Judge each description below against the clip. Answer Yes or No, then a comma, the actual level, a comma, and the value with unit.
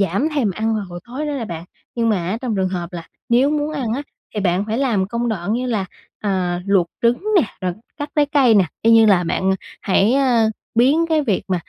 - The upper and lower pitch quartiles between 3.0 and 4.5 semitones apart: No, average, 5.2 semitones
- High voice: Yes, high, 220 Hz